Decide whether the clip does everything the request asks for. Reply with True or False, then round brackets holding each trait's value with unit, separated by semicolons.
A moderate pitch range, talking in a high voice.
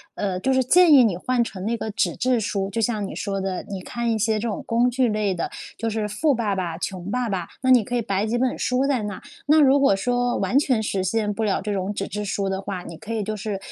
True (3.9 semitones; 215 Hz)